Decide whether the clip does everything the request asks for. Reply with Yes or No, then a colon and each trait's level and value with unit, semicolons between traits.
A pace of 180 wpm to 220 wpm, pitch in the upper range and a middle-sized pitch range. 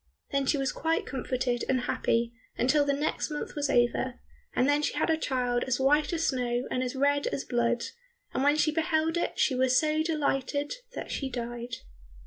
Yes: average, 195 wpm; very high, 270 Hz; average, 3.2 semitones